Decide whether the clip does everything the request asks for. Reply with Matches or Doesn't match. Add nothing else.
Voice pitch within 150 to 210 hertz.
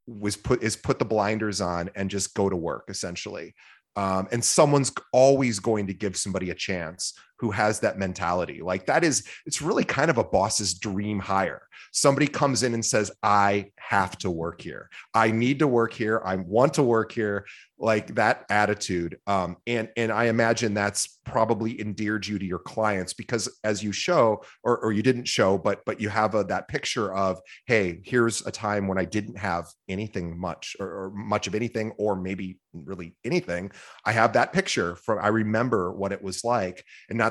Doesn't match